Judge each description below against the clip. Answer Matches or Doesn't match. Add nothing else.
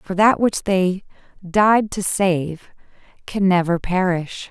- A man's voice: Doesn't match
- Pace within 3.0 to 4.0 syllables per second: Matches